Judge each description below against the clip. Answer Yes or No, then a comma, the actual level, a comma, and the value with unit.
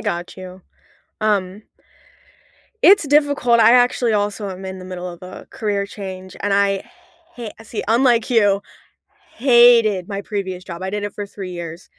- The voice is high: Yes, high, 200 Hz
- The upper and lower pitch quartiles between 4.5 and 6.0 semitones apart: No, average, 3.5 semitones